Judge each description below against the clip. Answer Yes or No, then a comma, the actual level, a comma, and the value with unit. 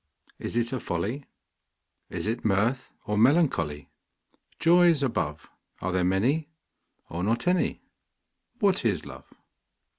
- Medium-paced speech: No, slow, 120 wpm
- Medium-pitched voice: No, low, 115 Hz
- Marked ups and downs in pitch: Yes, wide, 7.4 semitones